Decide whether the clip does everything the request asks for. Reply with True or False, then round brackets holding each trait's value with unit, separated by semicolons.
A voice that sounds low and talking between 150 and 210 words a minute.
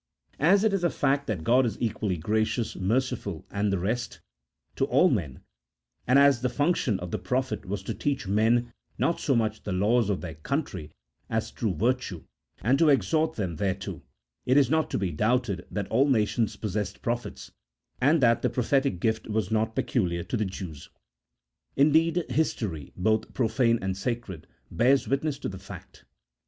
True (115 Hz; 175 wpm)